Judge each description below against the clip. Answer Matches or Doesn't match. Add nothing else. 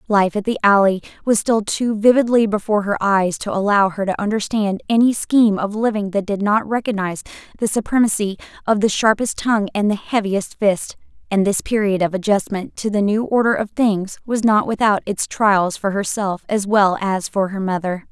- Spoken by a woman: Matches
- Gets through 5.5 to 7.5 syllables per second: Doesn't match